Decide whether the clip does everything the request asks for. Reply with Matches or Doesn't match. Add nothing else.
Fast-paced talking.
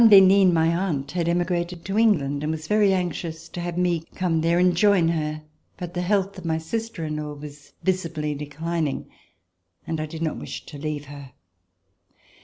Doesn't match